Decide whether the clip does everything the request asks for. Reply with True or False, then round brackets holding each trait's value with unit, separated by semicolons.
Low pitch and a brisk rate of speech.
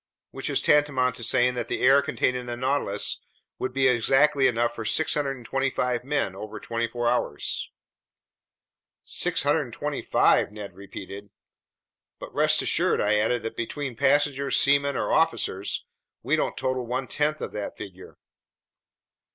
False (125 Hz; 140 wpm)